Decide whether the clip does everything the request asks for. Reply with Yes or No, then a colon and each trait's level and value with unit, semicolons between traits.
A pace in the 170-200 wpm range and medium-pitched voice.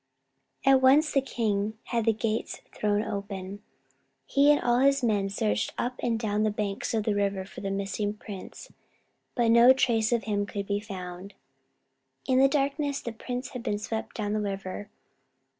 No: average, 175 wpm; high, 215 Hz